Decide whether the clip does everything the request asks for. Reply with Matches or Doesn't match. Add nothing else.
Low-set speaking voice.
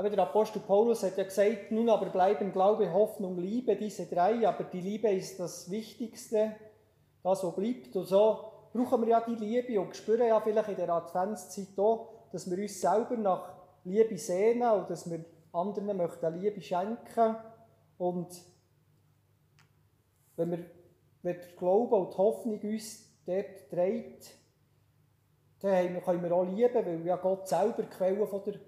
Doesn't match